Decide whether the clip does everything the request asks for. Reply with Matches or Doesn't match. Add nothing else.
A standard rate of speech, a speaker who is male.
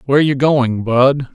Matches